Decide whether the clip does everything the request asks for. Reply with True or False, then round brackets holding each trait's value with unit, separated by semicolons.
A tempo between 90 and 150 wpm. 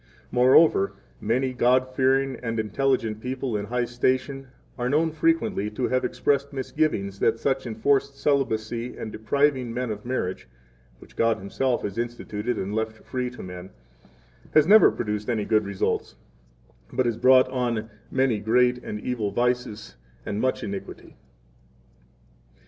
True (145 wpm)